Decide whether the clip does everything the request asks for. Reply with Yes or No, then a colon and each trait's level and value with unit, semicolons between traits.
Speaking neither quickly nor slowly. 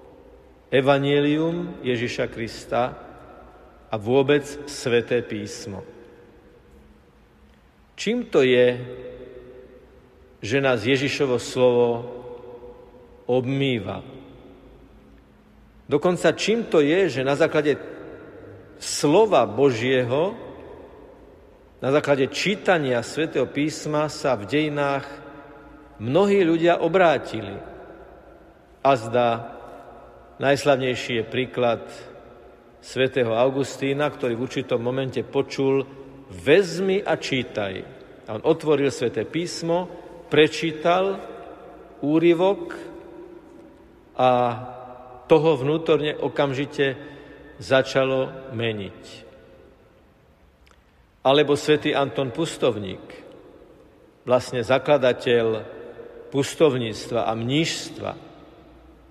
No: slow, 75 wpm